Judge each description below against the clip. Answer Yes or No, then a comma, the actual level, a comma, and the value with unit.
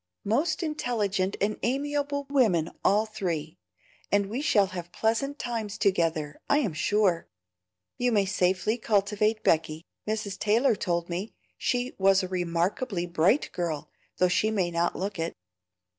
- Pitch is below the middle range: No, high, 200 Hz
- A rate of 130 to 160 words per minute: Yes, average, 145 wpm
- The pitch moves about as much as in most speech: Yes, average, 4.5 semitones